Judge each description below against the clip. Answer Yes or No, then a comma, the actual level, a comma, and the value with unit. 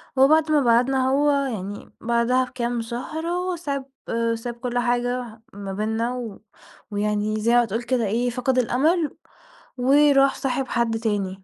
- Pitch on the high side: Yes, high, 245 Hz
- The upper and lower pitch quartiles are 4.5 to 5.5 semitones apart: No, average, 3.0 semitones